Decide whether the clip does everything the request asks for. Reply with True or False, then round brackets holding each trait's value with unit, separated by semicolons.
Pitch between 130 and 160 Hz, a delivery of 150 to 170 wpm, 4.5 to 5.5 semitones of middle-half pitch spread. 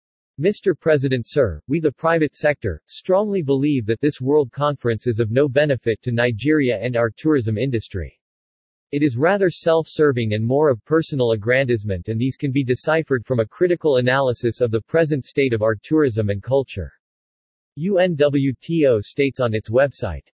True (135 Hz; 165 wpm; 4.8 semitones)